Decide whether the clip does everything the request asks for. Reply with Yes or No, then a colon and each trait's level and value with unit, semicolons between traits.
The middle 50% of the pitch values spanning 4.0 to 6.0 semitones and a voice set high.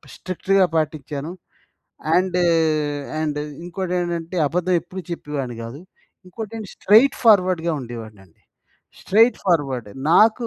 No: average, 4.5 semitones; medium, 175 Hz